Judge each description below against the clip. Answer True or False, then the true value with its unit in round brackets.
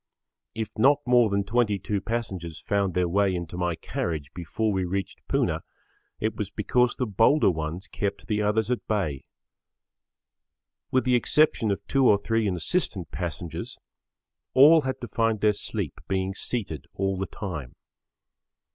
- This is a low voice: True (100 Hz)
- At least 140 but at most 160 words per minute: True (150 wpm)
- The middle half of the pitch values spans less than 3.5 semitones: False (4.2 semitones)